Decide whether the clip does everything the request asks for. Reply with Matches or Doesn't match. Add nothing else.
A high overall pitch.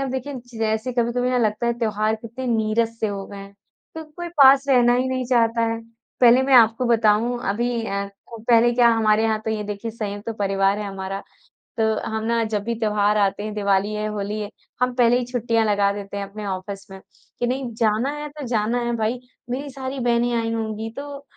Matches